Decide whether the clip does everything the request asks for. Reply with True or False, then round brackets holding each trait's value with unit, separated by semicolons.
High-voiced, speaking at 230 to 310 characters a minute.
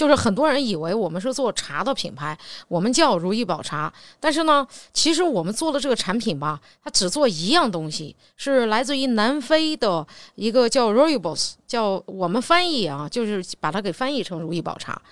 True (235 Hz; 305 characters per minute)